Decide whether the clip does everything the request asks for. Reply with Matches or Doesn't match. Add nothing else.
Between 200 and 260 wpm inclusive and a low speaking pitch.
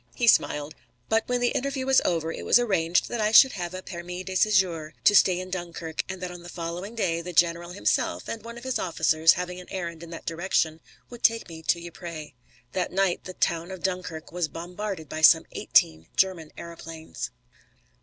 Doesn't match